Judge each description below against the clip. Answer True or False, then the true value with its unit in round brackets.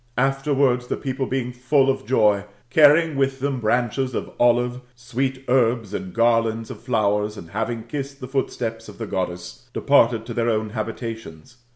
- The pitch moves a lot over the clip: False (3.0 semitones)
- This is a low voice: True (120 Hz)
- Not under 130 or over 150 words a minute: False (170 wpm)